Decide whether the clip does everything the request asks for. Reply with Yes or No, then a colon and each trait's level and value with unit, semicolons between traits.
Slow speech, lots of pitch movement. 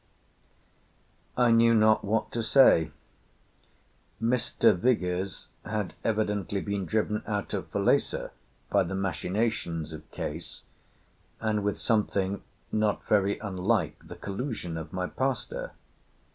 No: slow, 115 wpm; average, 3.1 semitones